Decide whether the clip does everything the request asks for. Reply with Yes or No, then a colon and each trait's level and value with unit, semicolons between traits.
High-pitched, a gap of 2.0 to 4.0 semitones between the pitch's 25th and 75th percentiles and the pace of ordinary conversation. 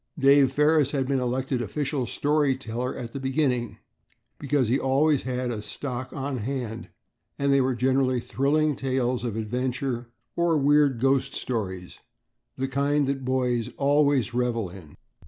No: low, 130 Hz; narrow, 2.4 semitones; average, 150 wpm